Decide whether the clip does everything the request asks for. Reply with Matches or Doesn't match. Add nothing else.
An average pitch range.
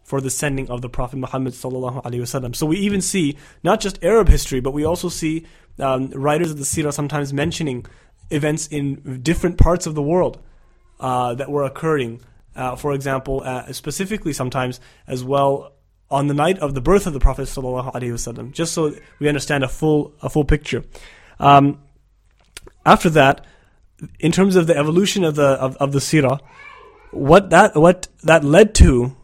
Matches